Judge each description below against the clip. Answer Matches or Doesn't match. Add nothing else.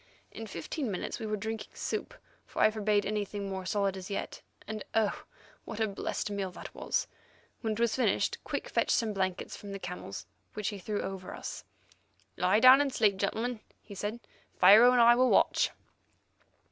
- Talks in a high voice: Matches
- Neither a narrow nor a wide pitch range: Doesn't match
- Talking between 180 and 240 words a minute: Matches